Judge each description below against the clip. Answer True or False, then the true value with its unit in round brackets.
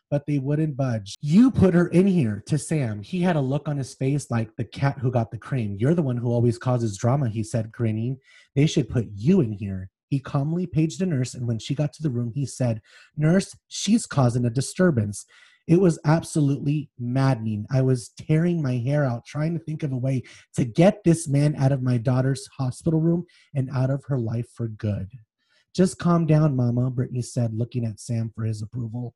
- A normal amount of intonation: True (4.6 semitones)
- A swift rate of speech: True (215 wpm)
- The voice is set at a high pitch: False (135 Hz)